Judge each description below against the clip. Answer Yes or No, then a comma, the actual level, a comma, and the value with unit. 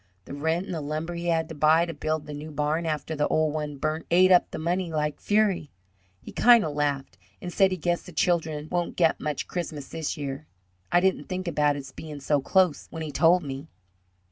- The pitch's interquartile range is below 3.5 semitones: Yes, average, 2.8 semitones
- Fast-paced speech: Yes, fast, 220 wpm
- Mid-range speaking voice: Yes, medium, 155 Hz